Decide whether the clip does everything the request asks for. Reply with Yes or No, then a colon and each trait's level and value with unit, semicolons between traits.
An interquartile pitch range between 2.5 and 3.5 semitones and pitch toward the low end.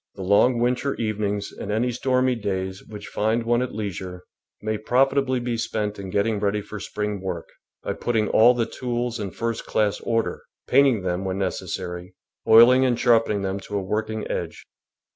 Yes: average, 3.1 semitones; low, 110 Hz